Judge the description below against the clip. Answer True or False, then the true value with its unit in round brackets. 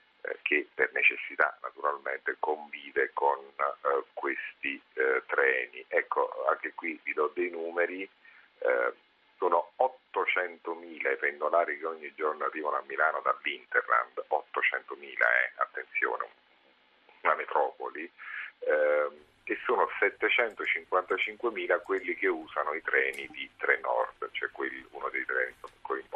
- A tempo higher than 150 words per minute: False (120 wpm)